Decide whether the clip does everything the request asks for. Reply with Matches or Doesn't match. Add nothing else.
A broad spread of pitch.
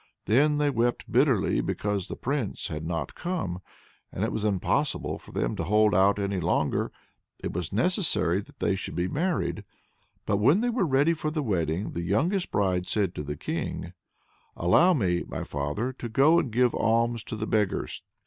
Matches